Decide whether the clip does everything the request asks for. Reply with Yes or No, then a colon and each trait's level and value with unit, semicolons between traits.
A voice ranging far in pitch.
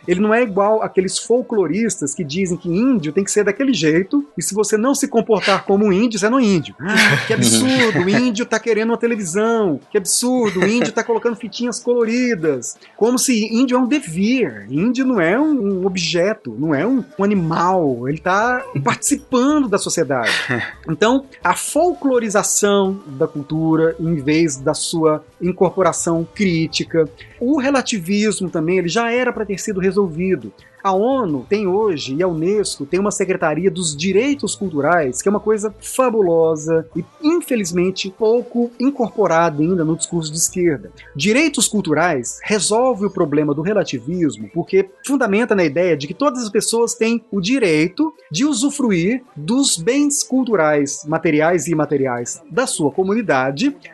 Yes: wide, 6.1 semitones